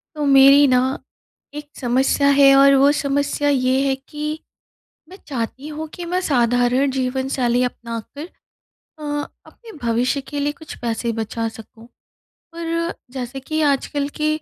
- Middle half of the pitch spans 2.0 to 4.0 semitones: Yes, average, 2.8 semitones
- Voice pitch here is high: Yes, very high, 275 Hz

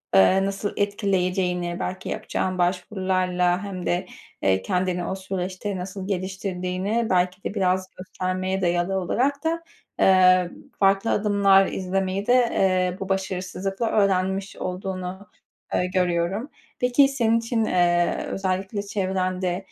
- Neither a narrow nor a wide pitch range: No, narrow, 1.4 semitones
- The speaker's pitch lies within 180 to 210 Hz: Yes, high, 190 Hz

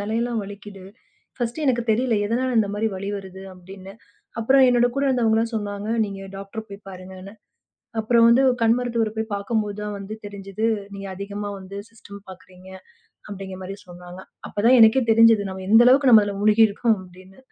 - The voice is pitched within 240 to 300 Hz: No, high, 210 Hz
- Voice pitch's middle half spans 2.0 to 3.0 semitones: Yes, average, 2.7 semitones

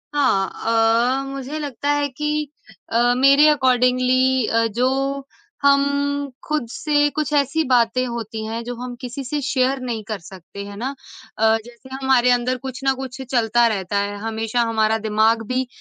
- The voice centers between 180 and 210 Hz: No, very high, 250 Hz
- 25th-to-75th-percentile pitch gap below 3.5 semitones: Yes, average, 3.1 semitones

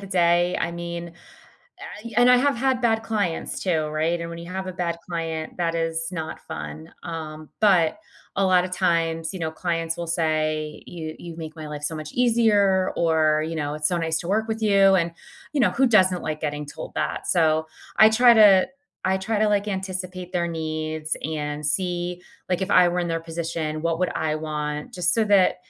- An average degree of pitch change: Yes, average, 3.1 semitones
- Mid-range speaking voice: Yes, medium, 170 Hz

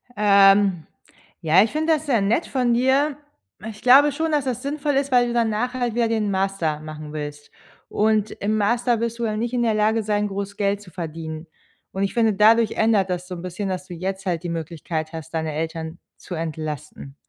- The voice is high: Yes, high, 205 Hz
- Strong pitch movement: Yes, wide, 5.7 semitones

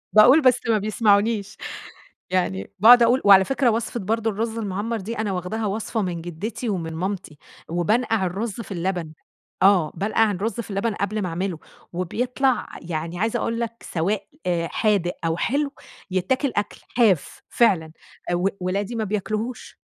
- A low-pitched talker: No, high, 205 Hz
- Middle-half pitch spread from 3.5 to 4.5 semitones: Yes, average, 3.9 semitones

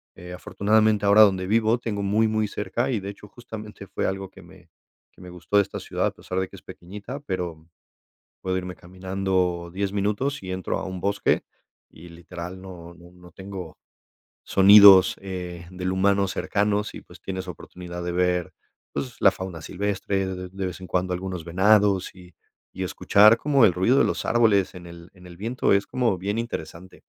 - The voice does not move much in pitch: Yes, narrow, 2.3 semitones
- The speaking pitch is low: Yes, very low, 95 Hz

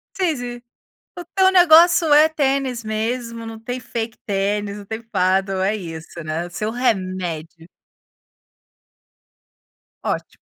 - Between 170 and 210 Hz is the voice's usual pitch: No, high, 225 Hz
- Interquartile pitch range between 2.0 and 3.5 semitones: No, average, 5.1 semitones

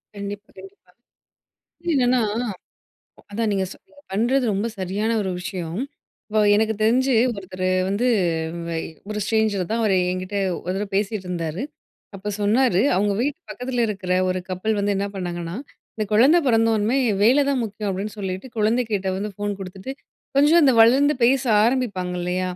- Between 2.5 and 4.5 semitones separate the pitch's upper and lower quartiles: Yes, average, 3.9 semitones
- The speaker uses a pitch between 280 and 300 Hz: No, high, 210 Hz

